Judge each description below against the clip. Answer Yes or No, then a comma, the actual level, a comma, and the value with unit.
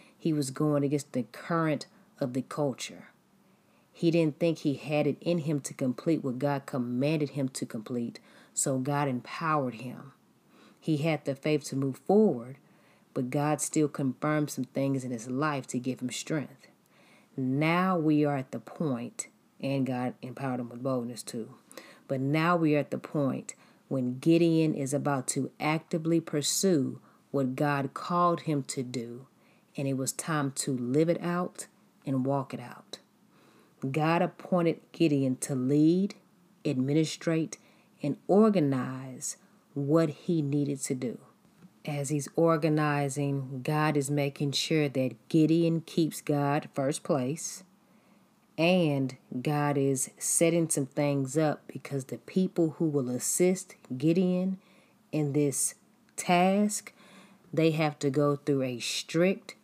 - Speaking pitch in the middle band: Yes, medium, 150 Hz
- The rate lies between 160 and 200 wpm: No, average, 145 wpm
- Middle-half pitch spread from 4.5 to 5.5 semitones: No, average, 3.7 semitones